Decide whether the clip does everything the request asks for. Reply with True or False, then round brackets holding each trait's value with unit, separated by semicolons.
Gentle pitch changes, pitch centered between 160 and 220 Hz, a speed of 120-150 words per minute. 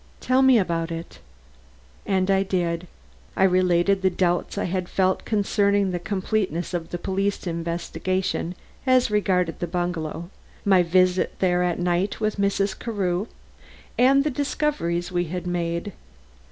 True (2.3 semitones; 185 Hz; 140 wpm)